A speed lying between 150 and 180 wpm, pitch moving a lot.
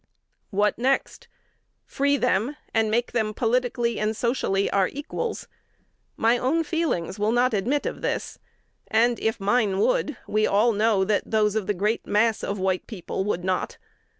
No: average, 160 wpm; average, 3.1 semitones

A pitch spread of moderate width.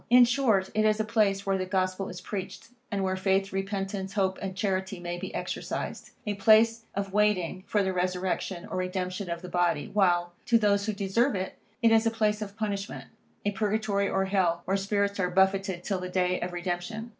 No: narrow, 2.2 semitones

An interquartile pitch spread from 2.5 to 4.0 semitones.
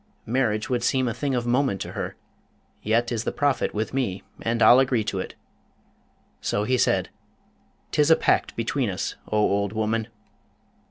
Yes: average, 3.3 semitones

